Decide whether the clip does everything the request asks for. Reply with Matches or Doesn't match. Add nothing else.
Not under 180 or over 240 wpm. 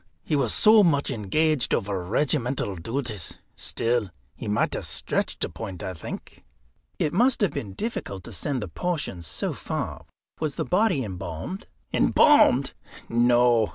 Doesn't match